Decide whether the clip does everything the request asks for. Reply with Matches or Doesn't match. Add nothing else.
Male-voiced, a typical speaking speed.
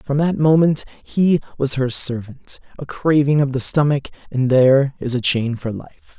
Matches